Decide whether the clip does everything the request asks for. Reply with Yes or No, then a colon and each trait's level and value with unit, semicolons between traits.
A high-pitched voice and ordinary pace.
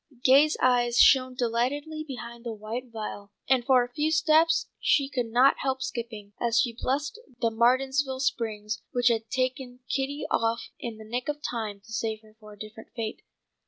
Yes: high, 245 Hz; average, 180 wpm